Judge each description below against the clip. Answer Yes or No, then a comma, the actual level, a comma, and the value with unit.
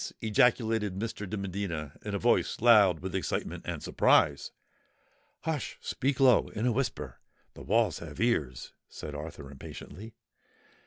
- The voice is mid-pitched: No, low, 105 Hz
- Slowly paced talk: Yes, slow, 125 wpm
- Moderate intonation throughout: No, wide, 5.8 semitones